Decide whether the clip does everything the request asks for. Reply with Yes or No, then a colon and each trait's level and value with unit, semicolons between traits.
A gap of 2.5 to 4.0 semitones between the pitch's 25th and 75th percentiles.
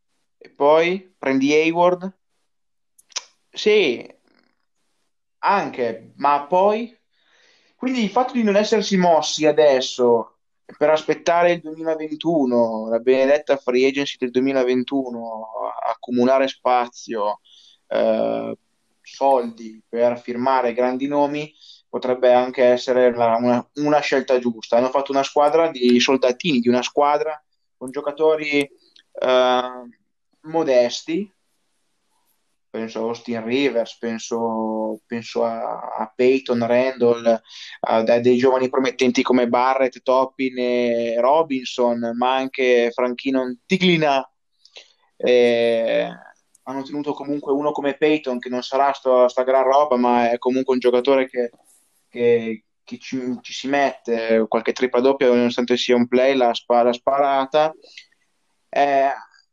Yes: average, 3.1 semitones